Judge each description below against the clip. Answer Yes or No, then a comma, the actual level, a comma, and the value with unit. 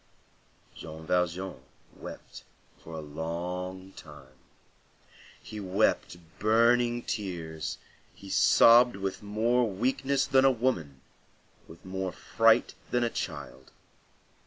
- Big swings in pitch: Yes, wide, 5.9 semitones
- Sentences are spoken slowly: Yes, slow, 105 wpm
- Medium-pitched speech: No, very low, 95 Hz